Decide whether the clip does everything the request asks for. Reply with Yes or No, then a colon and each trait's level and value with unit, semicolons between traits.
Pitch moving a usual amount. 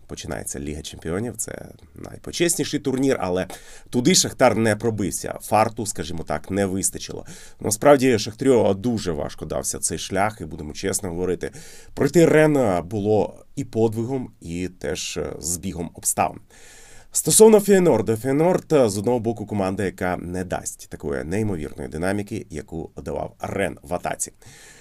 No: wide, 5.9 semitones